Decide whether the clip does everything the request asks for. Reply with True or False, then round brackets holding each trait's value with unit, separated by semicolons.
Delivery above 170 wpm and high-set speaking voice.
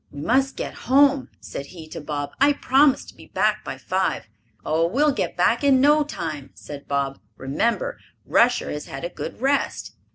True (185 wpm; 235 Hz)